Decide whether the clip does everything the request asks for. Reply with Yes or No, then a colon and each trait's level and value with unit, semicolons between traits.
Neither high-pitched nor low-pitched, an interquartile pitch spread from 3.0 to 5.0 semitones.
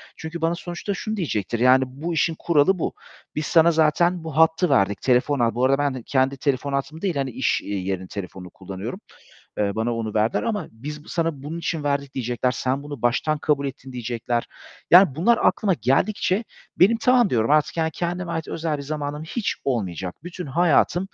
No: medium, 145 Hz; wide, 5.5 semitones